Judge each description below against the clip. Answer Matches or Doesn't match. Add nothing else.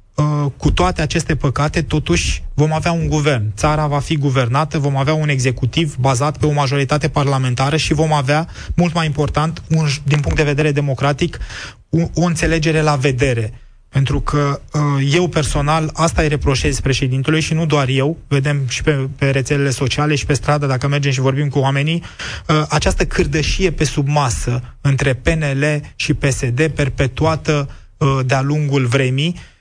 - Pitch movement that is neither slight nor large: Doesn't match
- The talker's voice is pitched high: Doesn't match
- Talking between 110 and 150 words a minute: Doesn't match